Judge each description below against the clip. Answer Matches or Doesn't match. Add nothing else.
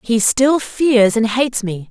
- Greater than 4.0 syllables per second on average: Doesn't match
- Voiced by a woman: Matches